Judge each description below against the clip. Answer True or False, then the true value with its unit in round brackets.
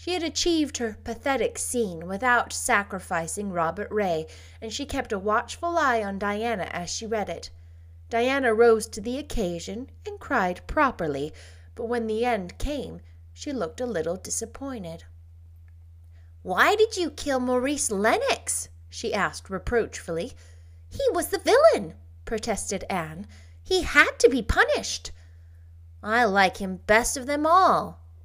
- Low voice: False (205 Hz)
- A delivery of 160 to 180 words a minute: False (140 wpm)